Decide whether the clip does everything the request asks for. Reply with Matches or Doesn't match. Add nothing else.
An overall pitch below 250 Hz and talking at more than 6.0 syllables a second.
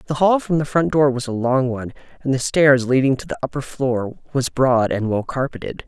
Doesn't match